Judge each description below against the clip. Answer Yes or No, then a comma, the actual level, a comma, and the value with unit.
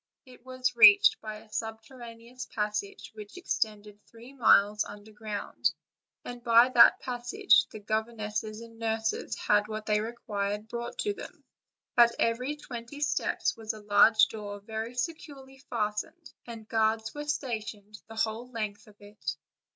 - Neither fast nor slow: Yes, average, 150 wpm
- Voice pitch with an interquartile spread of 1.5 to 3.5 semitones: Yes, narrow, 2.5 semitones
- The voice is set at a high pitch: Yes, high, 225 Hz